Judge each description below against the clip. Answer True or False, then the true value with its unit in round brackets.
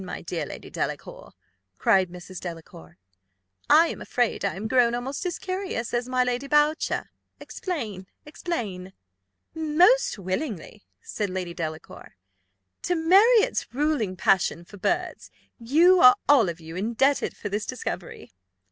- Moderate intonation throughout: False (8.6 semitones)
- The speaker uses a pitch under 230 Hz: False (235 Hz)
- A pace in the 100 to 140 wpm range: True (135 wpm)